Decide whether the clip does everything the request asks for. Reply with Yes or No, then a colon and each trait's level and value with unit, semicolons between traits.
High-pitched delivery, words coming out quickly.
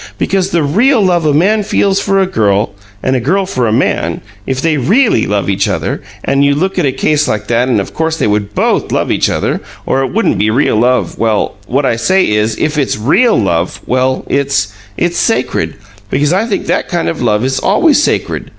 No: medium, 140 Hz; fast, 220 wpm